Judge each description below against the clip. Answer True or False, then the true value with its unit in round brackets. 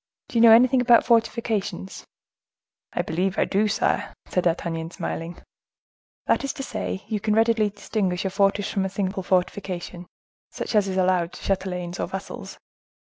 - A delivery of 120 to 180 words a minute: True (165 wpm)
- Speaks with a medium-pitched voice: False (195 Hz)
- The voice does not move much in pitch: False (3.3 semitones)